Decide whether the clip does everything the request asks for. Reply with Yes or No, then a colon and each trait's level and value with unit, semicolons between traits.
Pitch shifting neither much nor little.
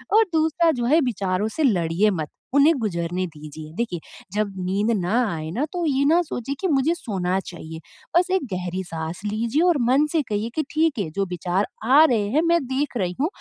No: wide, 8.8 semitones